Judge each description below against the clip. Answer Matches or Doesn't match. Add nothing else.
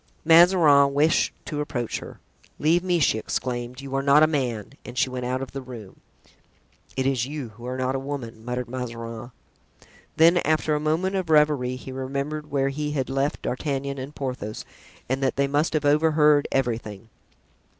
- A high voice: Doesn't match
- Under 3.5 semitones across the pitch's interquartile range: Matches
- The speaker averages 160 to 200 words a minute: Matches